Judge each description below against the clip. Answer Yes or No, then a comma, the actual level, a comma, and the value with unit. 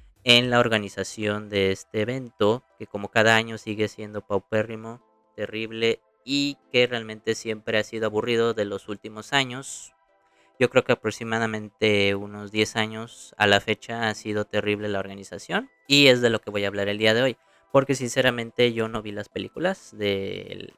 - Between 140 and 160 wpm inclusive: No, average, 175 wpm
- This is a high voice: No, low, 110 Hz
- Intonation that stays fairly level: Yes, narrow, 1.9 semitones